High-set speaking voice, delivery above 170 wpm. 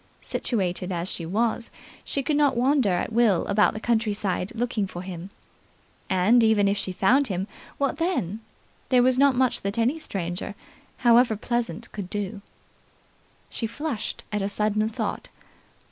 No: high, 215 Hz; average, 155 wpm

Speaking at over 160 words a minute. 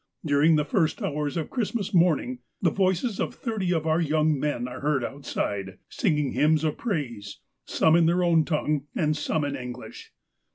Yes: average, 180 wpm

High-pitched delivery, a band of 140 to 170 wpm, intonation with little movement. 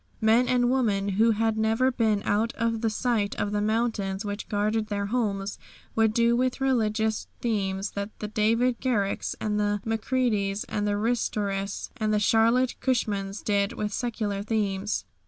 Yes: high, 215 Hz; average, 160 wpm; narrow, 2.1 semitones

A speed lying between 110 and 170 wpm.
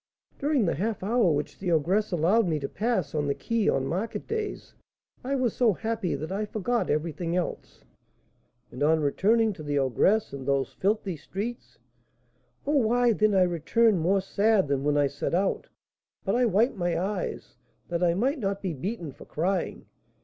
No: average, 180 wpm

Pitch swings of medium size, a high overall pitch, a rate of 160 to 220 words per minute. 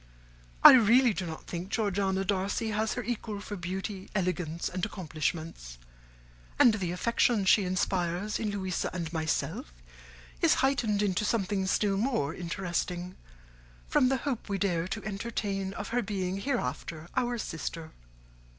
No: average, 3.3 semitones; high, 195 Hz; average, 140 wpm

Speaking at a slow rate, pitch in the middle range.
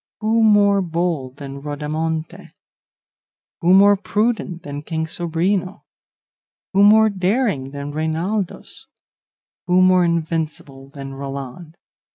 Yes: slow, 105 wpm; medium, 165 Hz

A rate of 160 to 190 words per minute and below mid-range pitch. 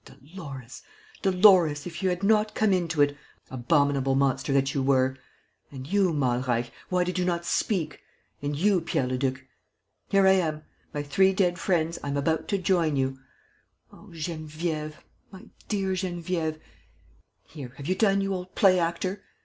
No: average, 165 wpm; medium, 165 Hz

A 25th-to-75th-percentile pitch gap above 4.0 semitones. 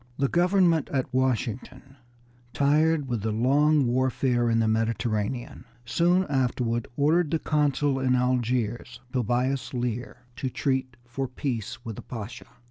No: average, 3.0 semitones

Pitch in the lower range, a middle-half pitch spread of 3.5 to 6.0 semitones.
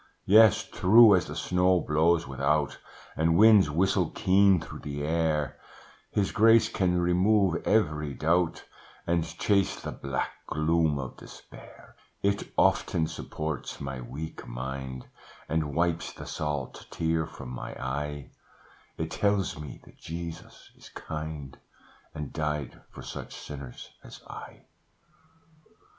Yes: very low, 80 Hz; average, 3.8 semitones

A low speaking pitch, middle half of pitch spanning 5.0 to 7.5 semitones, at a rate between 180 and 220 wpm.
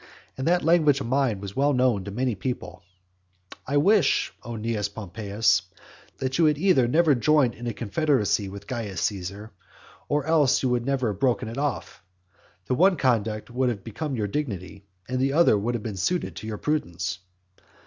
Yes: low, 120 Hz; wide, 5.5 semitones; average, 185 wpm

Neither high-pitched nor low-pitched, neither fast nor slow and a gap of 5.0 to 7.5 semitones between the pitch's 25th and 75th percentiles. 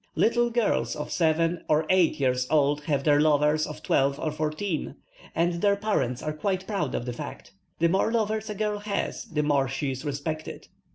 Yes: medium, 155 Hz; average, 190 wpm; wide, 5.4 semitones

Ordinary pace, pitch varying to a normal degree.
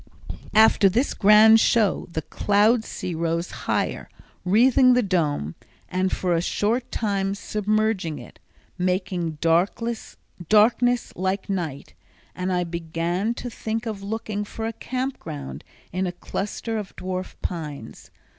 No: slow, 130 wpm; average, 4.1 semitones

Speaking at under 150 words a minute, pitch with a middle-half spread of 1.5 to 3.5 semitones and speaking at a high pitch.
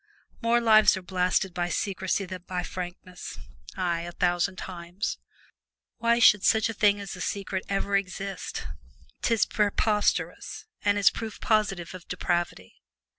Yes: average, 140 wpm; narrow, 2.5 semitones; high, 195 Hz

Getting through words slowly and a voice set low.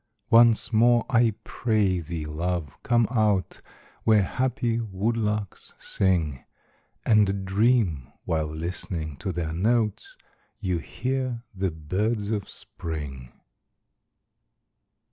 Yes: slow, 100 wpm; low, 100 Hz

